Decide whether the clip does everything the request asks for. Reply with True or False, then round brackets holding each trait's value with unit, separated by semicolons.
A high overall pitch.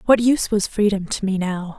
True (205 Hz)